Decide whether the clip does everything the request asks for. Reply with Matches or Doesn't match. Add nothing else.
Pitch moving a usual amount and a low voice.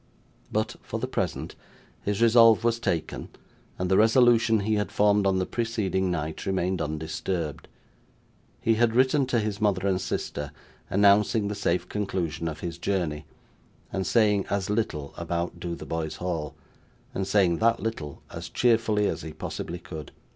Matches